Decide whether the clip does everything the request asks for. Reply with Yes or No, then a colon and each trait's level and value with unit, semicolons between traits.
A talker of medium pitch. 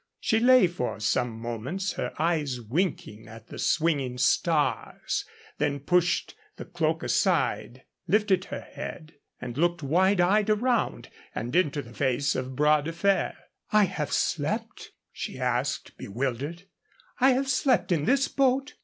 Yes: medium, 165 Hz